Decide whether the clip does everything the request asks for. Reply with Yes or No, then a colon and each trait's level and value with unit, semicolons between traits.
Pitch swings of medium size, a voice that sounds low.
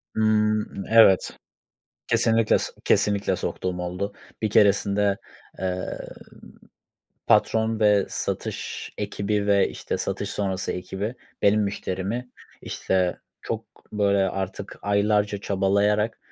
No: narrow, 1.7 semitones; low, 100 Hz